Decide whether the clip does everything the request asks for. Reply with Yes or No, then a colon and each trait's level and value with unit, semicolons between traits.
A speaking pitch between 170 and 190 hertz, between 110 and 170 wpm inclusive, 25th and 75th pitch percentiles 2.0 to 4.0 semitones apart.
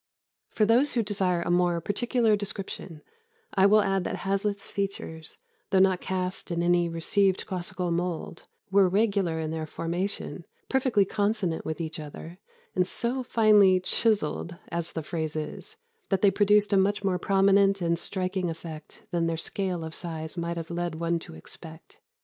Yes: medium, 185 Hz; average, 165 wpm; average, 3.1 semitones